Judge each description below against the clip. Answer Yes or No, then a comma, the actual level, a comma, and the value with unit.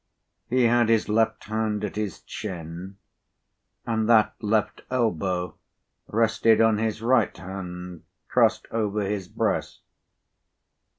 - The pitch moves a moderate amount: Yes, average, 3.0 semitones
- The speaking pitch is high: No, low, 105 Hz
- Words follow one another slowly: Yes, slow, 115 wpm